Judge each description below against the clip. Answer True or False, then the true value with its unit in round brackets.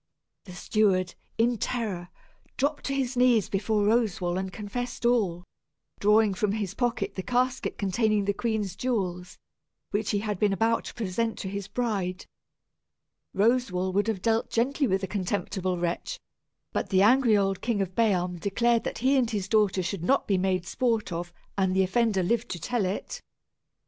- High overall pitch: True (205 Hz)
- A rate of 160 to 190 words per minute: True (170 wpm)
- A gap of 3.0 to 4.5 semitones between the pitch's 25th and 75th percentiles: True (3.6 semitones)